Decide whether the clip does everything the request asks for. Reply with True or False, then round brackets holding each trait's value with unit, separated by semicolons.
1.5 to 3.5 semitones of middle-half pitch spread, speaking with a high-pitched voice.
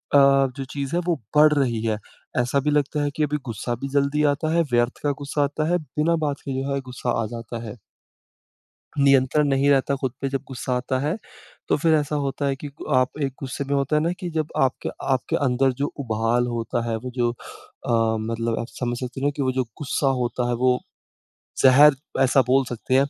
False (2.8 semitones; 135 Hz)